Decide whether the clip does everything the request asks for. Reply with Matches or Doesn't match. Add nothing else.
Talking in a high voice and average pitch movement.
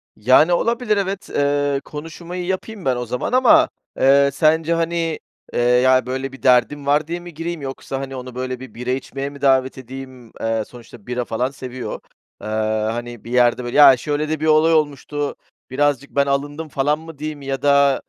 Doesn't match